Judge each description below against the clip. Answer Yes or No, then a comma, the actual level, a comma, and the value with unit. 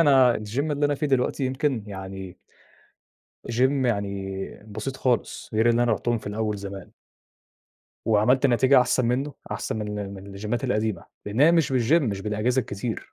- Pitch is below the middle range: Yes, low, 115 Hz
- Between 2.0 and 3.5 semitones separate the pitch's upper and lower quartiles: No, average, 4.2 semitones